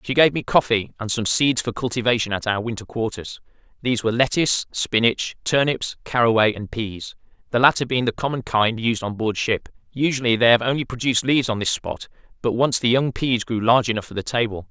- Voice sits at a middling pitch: No, low, 120 Hz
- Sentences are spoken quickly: Yes, fast, 210 wpm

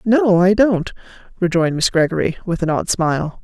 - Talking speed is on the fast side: No, average, 175 wpm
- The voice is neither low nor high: Yes, medium, 180 Hz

